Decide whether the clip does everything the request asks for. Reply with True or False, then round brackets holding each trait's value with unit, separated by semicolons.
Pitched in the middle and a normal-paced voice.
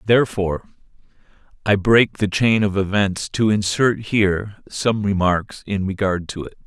False (100 Hz; 145 wpm)